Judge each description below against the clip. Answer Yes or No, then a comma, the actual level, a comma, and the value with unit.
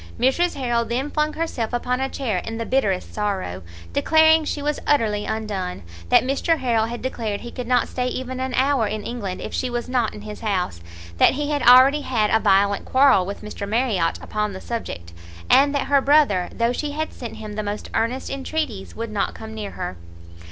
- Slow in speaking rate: No, fast, 205 wpm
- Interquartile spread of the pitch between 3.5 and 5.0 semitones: Yes, average, 4.4 semitones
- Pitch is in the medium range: No, high, 235 Hz